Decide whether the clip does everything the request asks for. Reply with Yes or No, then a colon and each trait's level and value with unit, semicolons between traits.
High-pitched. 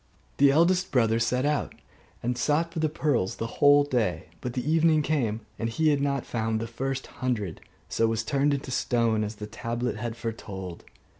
No: low, 125 Hz